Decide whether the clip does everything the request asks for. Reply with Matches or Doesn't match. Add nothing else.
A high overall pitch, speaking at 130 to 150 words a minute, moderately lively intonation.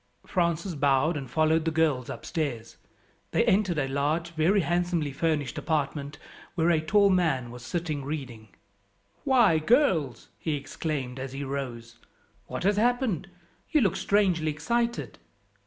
Doesn't match